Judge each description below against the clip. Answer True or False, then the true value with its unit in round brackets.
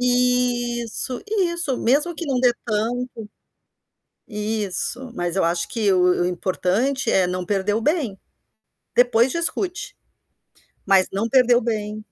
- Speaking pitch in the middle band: False (235 Hz)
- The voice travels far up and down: False (4.3 semitones)